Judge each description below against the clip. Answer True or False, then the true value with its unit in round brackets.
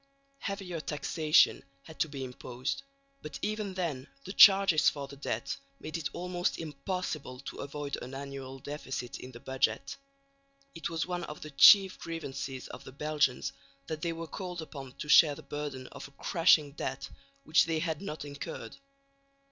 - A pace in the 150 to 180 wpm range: True (165 wpm)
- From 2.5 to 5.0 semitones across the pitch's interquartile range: True (3.3 semitones)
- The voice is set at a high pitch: False (150 Hz)